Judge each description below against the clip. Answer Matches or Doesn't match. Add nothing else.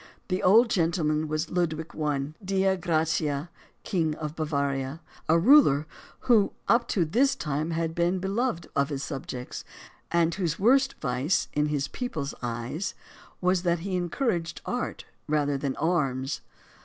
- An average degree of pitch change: Matches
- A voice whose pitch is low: Doesn't match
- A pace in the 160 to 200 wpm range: Doesn't match